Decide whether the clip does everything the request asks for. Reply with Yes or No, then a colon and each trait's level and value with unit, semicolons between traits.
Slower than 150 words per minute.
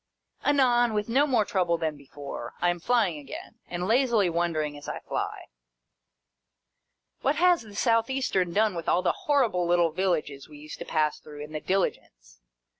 No: average, 175 wpm